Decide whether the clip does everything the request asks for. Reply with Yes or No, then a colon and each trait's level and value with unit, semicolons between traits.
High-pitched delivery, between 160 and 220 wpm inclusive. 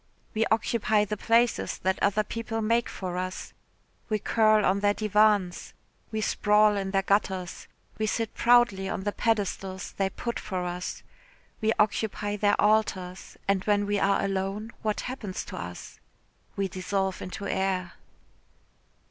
No: high, 205 Hz; average, 150 wpm